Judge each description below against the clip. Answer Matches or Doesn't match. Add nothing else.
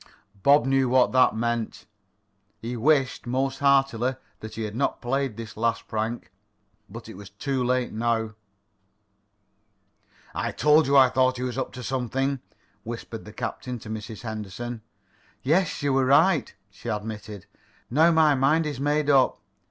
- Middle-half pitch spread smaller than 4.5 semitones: Matches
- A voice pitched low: Matches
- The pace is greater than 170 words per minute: Doesn't match